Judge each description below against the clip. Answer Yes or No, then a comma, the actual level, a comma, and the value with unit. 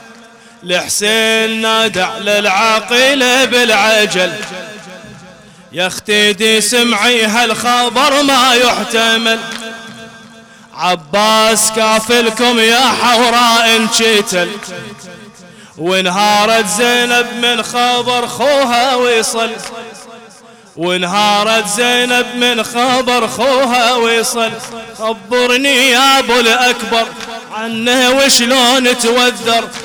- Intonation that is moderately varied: No, narrow, 1.9 semitones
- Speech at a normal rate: No, slow, 70 wpm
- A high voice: Yes, high, 230 Hz